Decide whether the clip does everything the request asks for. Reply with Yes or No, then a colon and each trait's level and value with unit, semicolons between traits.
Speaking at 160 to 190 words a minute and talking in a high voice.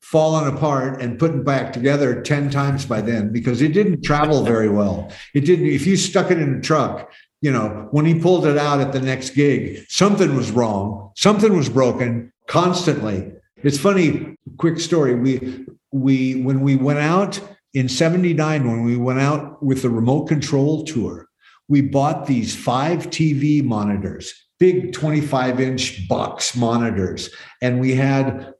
No: average, 165 wpm; medium, 140 Hz